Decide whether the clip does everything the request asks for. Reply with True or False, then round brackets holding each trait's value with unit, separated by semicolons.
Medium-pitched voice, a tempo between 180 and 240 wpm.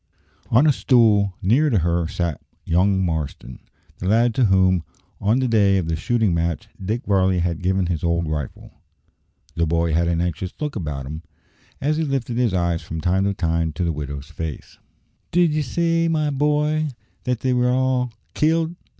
False (95 Hz; 185 wpm)